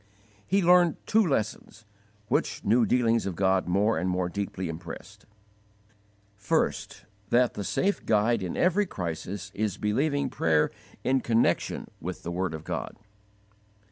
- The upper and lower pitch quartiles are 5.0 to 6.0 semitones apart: Yes, wide, 5.5 semitones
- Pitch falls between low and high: No, low, 105 Hz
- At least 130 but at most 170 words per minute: Yes, average, 140 wpm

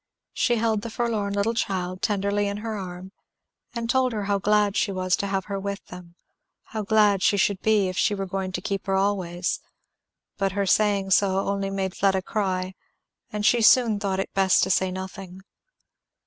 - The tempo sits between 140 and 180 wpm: No, average, 190 wpm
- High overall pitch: Yes, high, 200 Hz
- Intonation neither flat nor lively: No, narrow, 1.7 semitones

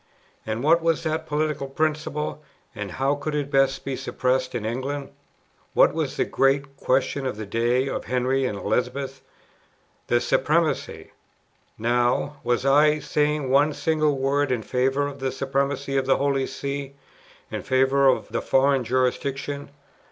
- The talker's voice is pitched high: No, low, 135 Hz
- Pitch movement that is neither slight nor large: No, narrow, 1.9 semitones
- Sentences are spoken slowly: No, average, 150 wpm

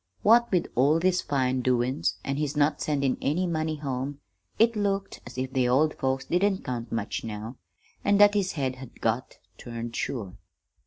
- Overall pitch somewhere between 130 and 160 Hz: Yes, low, 135 Hz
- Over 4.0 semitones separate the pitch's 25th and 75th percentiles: Yes, wide, 5.6 semitones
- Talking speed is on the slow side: No, average, 175 wpm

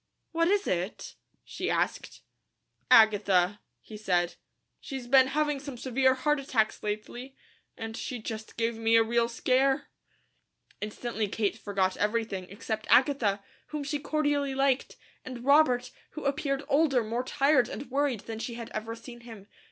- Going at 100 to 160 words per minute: Yes, average, 150 wpm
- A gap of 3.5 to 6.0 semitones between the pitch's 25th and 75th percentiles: Yes, average, 4.1 semitones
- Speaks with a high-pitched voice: Yes, high, 240 Hz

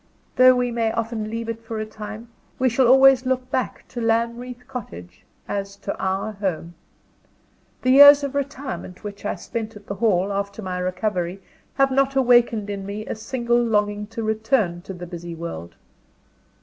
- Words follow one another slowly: No, average, 175 wpm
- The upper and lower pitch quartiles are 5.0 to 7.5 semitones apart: No, average, 3.9 semitones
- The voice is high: Yes, high, 220 Hz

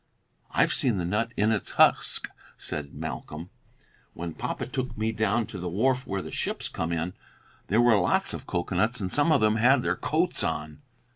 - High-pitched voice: No, low, 105 Hz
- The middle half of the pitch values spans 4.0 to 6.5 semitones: Yes, wide, 5.6 semitones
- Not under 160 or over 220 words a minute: Yes, average, 190 wpm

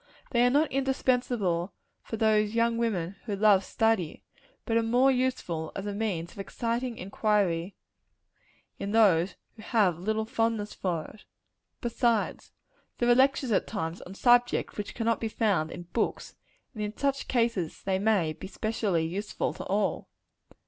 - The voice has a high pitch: Yes, high, 215 Hz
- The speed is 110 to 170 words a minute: Yes, average, 160 wpm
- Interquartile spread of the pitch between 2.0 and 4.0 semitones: Yes, average, 3.7 semitones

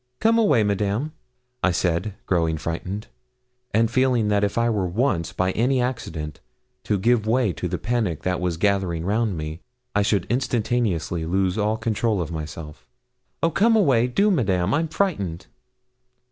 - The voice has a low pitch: Yes, low, 105 Hz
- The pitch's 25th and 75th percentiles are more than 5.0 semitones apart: Yes, wide, 5.5 semitones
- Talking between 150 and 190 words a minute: Yes, average, 160 wpm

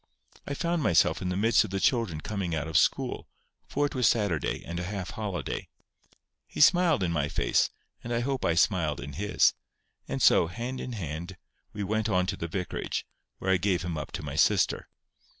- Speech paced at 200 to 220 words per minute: Yes, fast, 205 wpm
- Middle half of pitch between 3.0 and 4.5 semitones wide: No, average, 5.3 semitones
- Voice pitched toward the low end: Yes, very low, 95 Hz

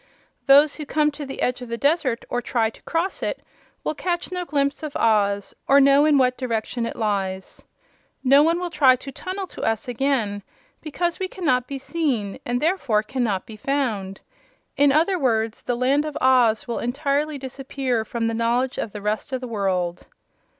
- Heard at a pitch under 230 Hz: No, very high, 260 Hz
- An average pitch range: Yes, average, 4.5 semitones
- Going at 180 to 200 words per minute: Yes, average, 190 wpm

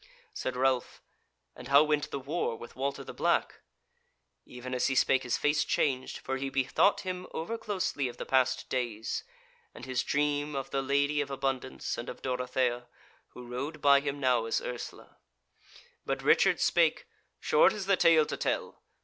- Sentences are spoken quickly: No, average, 175 wpm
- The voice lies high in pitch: No, low, 135 Hz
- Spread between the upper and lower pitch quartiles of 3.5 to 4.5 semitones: No, narrow, 2.5 semitones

